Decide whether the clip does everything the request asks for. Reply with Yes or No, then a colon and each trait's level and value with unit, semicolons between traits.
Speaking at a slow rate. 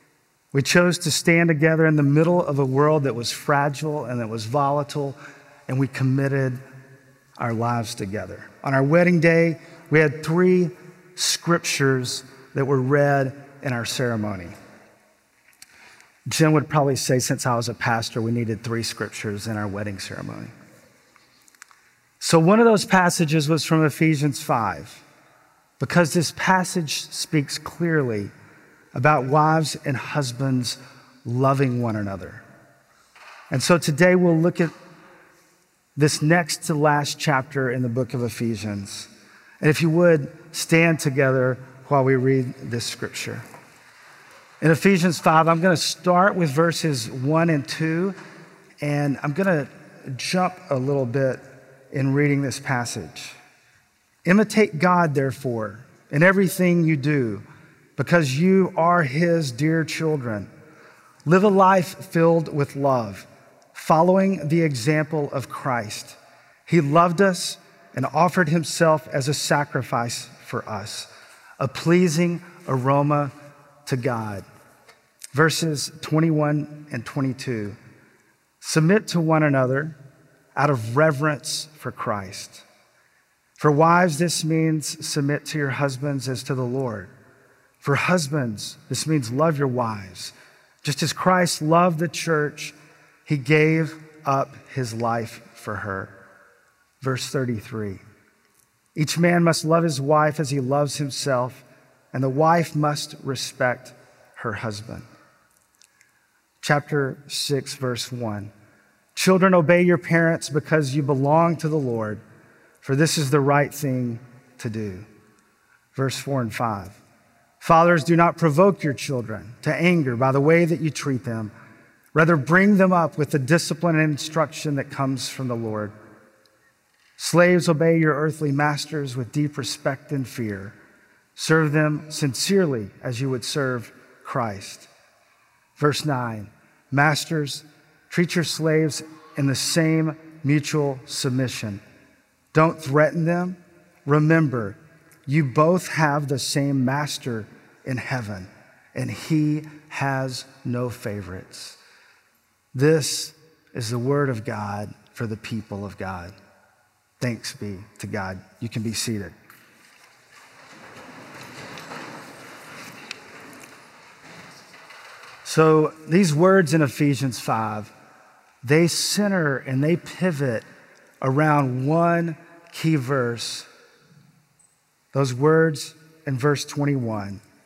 Yes: slow, 125 wpm